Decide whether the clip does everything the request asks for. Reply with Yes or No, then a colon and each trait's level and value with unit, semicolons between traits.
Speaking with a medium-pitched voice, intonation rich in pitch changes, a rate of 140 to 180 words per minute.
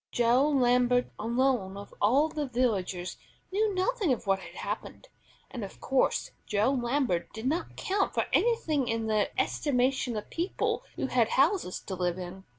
No: high, 245 Hz; wide, 5.7 semitones; average, 160 wpm